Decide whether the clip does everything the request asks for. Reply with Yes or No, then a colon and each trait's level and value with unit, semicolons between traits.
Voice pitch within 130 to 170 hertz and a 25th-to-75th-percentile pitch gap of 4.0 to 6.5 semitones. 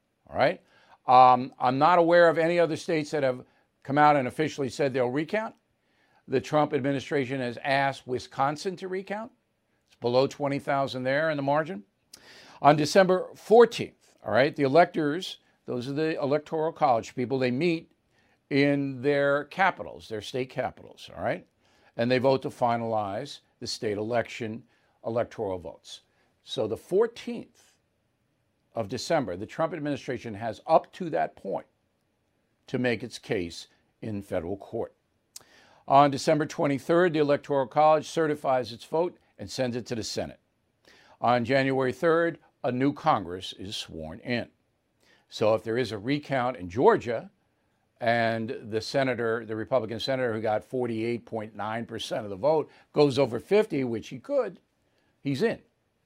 Yes: low, 135 Hz; average, 4.6 semitones